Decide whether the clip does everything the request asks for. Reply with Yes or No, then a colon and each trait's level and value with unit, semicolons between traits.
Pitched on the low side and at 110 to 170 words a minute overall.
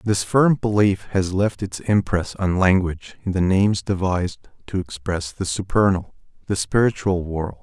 Yes: very low, 95 Hz; average, 155 wpm